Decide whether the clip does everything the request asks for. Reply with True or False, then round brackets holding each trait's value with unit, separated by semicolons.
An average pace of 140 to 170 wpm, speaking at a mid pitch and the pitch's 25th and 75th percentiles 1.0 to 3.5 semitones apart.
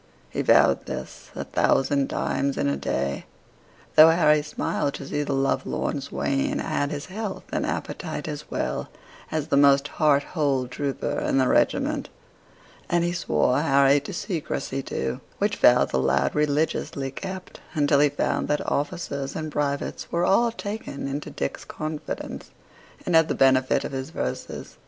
True (160 wpm; 145 Hz; 2.4 semitones)